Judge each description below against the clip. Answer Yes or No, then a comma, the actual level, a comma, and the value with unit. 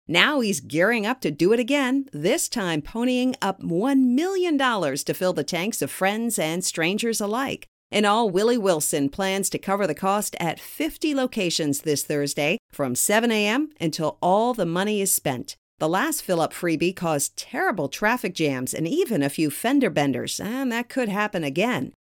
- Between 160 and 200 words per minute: Yes, average, 180 wpm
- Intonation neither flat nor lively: No, wide, 7.2 semitones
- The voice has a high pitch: Yes, high, 195 Hz